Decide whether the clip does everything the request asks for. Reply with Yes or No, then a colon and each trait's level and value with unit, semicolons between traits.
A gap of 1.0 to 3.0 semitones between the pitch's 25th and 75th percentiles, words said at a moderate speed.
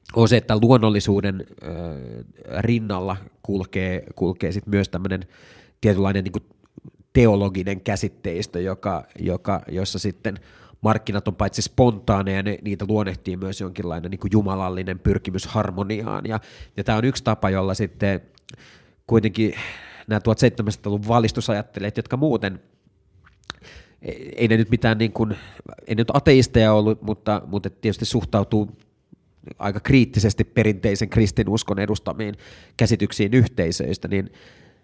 Yes: narrow, 2.5 semitones; average, 120 wpm